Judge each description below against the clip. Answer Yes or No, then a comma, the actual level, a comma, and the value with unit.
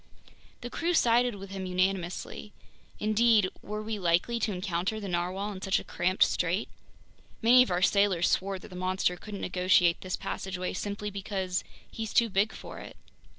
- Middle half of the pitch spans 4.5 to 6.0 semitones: No, average, 2.7 semitones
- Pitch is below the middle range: No, high, 195 Hz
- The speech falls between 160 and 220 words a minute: Yes, average, 170 wpm